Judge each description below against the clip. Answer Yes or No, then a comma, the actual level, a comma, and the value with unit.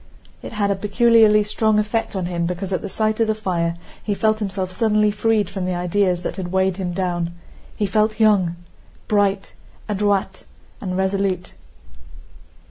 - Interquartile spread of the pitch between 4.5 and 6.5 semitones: No, narrow, 2.6 semitones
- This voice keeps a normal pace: Yes, average, 165 wpm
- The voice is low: No, high, 200 Hz